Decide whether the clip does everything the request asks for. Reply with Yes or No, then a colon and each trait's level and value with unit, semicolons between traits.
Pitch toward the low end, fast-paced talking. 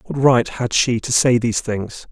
Yes: low, 120 Hz; fast, 225 wpm